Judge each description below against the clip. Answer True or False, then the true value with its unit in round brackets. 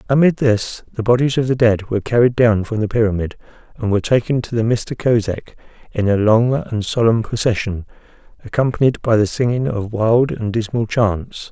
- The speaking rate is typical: True (180 wpm)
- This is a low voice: True (115 Hz)